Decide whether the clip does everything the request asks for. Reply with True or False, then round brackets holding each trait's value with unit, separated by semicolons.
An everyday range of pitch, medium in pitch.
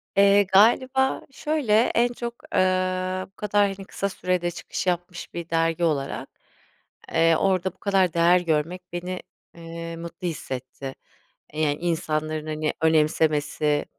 True (3.3 semitones; 175 Hz)